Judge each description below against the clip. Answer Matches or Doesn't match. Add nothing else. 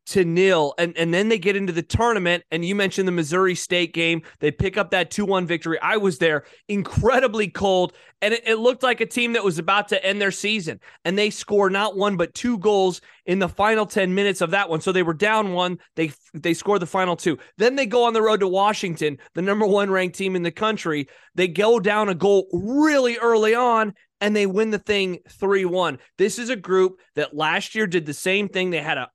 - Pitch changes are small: Doesn't match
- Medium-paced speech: Doesn't match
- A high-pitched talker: Matches